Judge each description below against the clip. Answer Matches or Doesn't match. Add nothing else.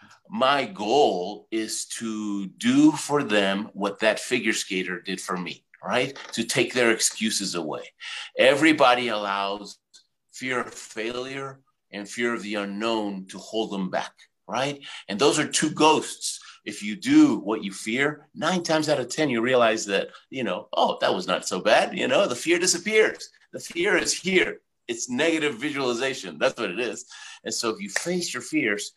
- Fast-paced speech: Doesn't match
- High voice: Doesn't match